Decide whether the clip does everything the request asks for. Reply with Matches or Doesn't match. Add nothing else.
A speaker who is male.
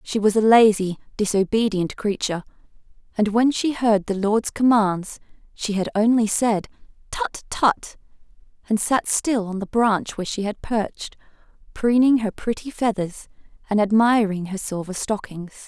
Doesn't match